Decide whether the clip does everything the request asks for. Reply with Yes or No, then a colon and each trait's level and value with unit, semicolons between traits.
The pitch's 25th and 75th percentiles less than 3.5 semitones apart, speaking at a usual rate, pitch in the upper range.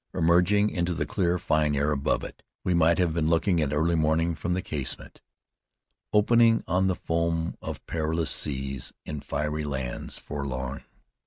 No: average, 2.9 semitones; average, 160 wpm; very low, 80 Hz